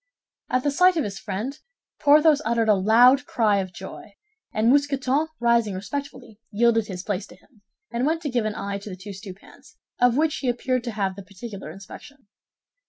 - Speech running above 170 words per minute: Yes, average, 190 wpm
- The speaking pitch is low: No, high, 235 Hz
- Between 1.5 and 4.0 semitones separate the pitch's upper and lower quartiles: No, wide, 5.4 semitones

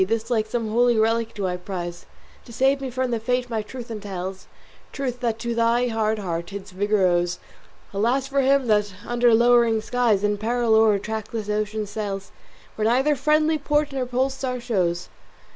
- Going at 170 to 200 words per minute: Yes, average, 185 wpm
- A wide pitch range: No, average, 3.2 semitones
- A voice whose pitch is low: No, high, 225 Hz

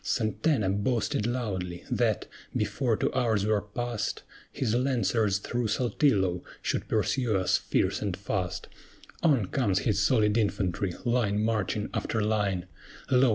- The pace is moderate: No, slow, 130 wpm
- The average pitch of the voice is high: No, low, 110 Hz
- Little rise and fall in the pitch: No, average, 3.3 semitones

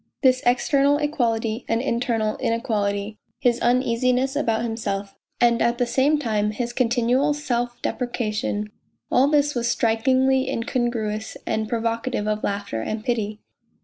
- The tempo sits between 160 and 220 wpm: No, slow, 135 wpm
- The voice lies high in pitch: Yes, high, 235 Hz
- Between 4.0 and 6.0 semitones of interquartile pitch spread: No, average, 2.7 semitones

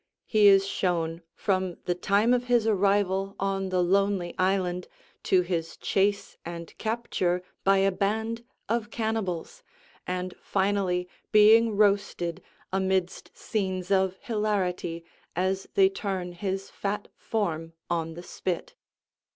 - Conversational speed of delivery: No, slow, 125 wpm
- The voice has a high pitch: Yes, high, 195 Hz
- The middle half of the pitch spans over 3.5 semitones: No, narrow, 2.6 semitones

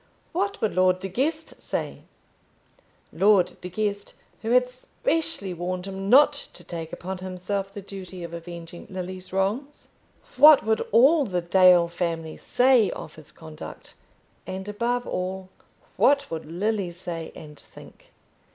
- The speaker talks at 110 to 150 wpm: Yes, average, 140 wpm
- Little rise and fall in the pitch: No, average, 4.5 semitones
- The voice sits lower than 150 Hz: No, high, 190 Hz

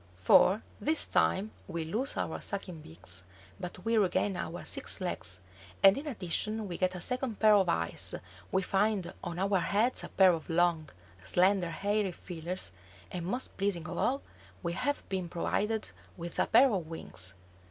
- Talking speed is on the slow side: No, average, 170 wpm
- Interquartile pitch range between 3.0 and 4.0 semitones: Yes, average, 3.7 semitones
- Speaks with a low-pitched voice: No, medium, 185 Hz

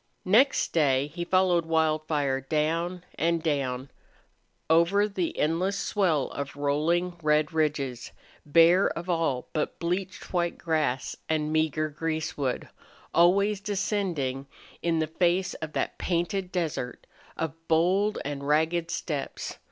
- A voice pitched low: No, medium, 165 Hz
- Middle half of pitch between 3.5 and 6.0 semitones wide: No, average, 3.0 semitones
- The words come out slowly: Yes, slow, 120 wpm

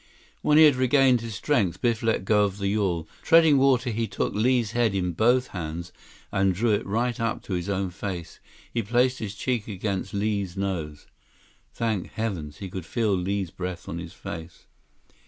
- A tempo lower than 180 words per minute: No, average, 185 wpm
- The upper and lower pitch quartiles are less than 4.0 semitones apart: No, average, 4.3 semitones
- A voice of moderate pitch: No, low, 100 Hz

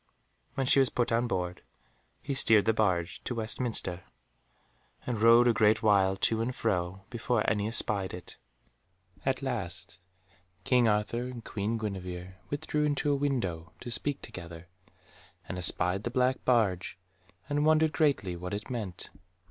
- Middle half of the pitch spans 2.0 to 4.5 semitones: No, average, 5.1 semitones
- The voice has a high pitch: No, low, 110 Hz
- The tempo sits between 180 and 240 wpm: No, average, 150 wpm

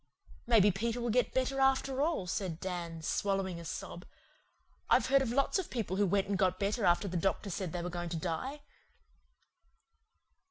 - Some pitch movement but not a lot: No, wide, 5.8 semitones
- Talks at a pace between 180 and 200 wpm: Yes, average, 185 wpm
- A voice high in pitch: Yes, high, 195 Hz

